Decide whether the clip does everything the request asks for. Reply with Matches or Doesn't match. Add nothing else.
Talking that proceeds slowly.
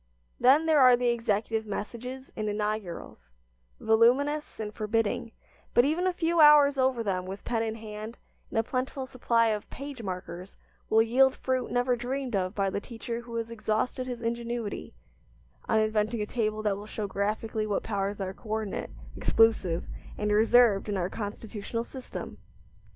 Doesn't match